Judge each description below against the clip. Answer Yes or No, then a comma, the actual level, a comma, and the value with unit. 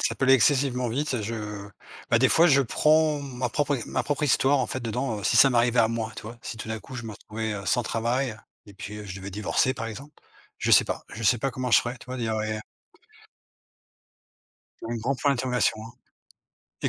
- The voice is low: Yes, low, 120 Hz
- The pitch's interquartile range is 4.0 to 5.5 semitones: No, average, 3.2 semitones